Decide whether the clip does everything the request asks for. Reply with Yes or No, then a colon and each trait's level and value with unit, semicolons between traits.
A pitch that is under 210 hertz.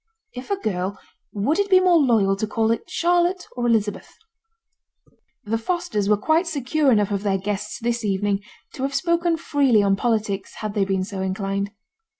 No: high, 225 Hz